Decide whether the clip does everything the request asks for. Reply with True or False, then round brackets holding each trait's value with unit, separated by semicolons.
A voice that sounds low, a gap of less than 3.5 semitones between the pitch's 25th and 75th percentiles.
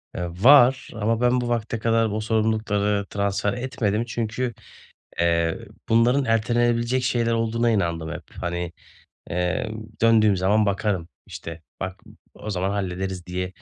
False (110 Hz; 3.8 semitones)